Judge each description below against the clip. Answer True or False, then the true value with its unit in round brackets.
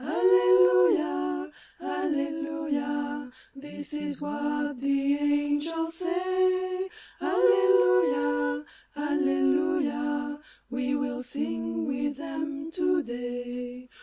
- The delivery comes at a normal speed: False (75 wpm)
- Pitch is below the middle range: False (285 Hz)